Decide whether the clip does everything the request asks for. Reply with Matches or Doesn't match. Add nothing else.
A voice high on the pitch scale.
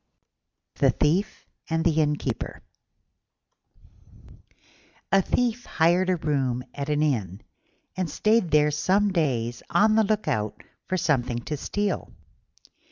Doesn't match